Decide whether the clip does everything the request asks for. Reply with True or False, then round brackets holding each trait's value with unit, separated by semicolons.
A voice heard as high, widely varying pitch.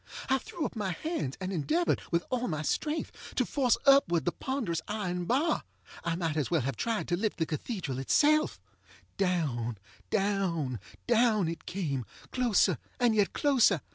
True (195 Hz; 7.1 semitones)